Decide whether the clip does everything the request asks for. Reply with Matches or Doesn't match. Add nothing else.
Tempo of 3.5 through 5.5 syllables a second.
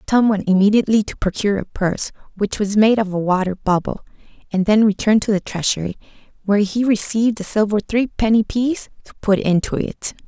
Doesn't match